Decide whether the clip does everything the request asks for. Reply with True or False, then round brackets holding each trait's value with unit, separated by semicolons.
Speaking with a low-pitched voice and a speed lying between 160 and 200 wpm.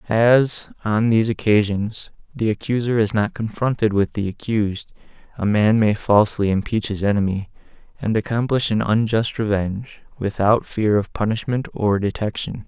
False (110 Hz; 140 wpm)